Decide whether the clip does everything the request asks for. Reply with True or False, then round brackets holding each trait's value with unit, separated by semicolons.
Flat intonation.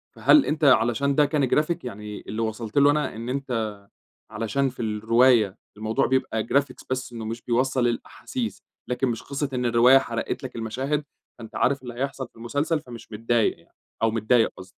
False (3.4 semitones)